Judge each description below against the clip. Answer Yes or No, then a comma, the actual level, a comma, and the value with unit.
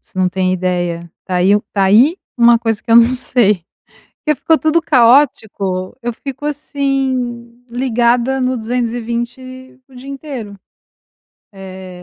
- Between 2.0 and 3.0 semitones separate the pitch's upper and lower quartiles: No, average, 4.5 semitones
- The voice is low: No, high, 240 Hz